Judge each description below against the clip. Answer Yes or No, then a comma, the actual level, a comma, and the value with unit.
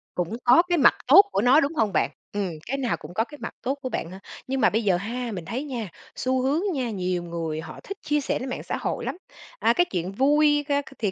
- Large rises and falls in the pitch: Yes, wide, 6.6 semitones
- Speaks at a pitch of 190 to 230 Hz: No, high, 245 Hz